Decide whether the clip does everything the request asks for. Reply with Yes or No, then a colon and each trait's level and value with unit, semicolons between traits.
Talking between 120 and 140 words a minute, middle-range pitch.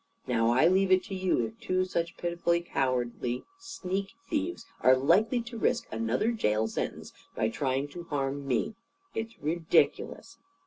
No: average, 150 wpm; medium, 170 Hz